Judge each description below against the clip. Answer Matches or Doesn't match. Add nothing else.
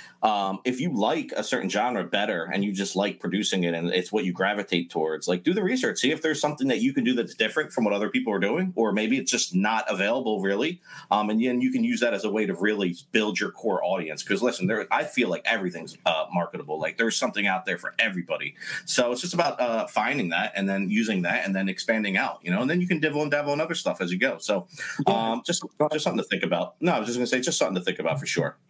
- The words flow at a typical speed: Doesn't match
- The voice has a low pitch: Matches